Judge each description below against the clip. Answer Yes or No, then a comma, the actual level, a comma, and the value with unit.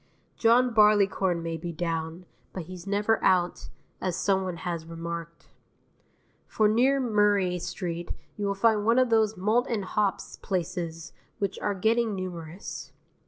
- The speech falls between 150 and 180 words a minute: No, average, 140 wpm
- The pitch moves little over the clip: No, average, 3.8 semitones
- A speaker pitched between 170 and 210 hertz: Yes, high, 190 Hz